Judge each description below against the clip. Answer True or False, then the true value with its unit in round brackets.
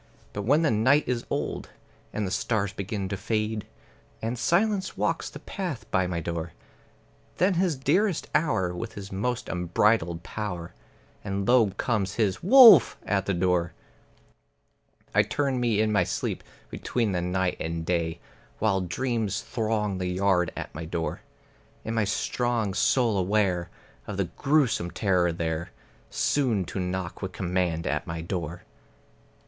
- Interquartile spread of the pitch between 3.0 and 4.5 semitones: False (5.1 semitones)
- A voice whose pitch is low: True (100 Hz)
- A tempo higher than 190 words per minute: False (150 wpm)